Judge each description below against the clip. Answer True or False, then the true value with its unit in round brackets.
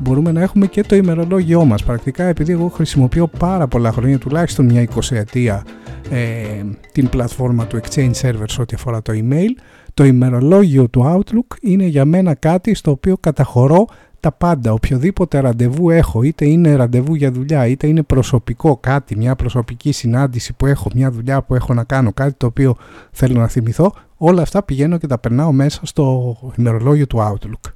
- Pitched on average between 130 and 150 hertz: True (135 Hz)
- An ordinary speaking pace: False (175 wpm)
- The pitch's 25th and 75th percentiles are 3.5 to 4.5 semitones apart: False (4.9 semitones)